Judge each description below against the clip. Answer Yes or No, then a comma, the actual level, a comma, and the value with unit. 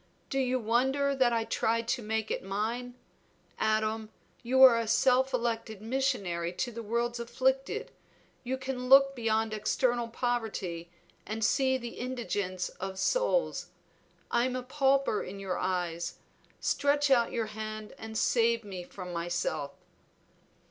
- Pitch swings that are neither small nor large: Yes, average, 3.4 semitones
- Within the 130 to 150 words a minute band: Yes, average, 140 wpm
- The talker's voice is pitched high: Yes, high, 235 Hz